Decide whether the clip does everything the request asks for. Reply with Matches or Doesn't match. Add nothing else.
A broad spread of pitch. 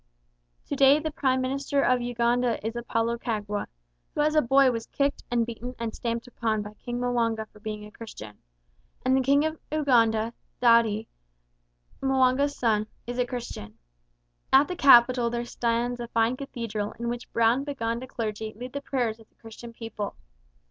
Doesn't match